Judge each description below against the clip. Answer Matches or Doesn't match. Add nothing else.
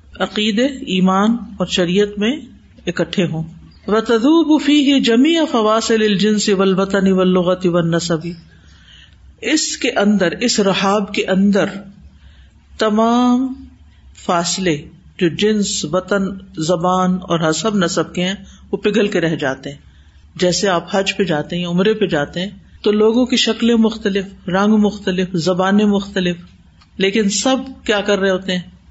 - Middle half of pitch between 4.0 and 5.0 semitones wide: Doesn't match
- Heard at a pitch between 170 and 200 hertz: Matches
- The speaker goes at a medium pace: Matches